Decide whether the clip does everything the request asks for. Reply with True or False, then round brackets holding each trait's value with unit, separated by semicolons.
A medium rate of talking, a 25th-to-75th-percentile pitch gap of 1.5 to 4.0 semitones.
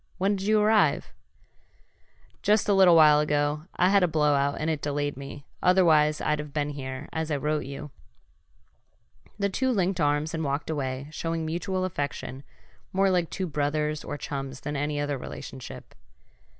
True (165 wpm; 3.7 semitones)